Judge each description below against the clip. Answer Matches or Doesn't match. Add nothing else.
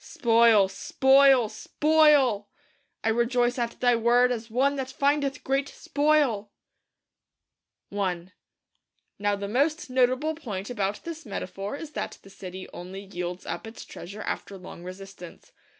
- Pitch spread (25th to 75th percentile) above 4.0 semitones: Matches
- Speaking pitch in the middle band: Doesn't match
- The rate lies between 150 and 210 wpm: Doesn't match